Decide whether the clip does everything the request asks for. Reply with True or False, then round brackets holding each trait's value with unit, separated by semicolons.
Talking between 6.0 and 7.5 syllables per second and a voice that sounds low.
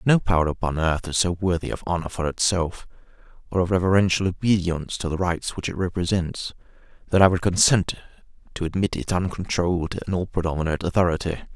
True (6.2 syllables/s; 90 Hz)